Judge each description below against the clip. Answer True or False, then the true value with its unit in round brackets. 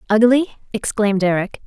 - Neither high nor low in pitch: False (220 Hz)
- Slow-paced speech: True (110 wpm)